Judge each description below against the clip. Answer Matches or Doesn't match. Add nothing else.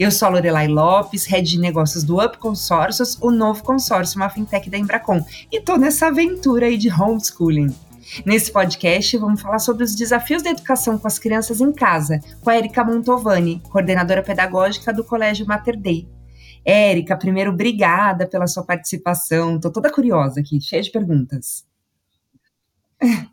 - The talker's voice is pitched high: Matches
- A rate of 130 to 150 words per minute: Doesn't match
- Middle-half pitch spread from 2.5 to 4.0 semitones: Doesn't match